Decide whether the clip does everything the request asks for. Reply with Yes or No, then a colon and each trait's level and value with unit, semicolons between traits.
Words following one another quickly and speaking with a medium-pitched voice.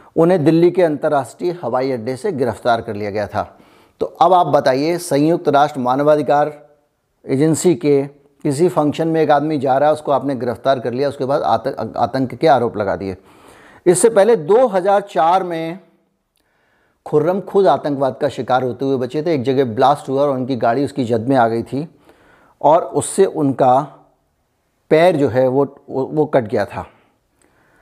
No: average, 175 wpm; medium, 145 Hz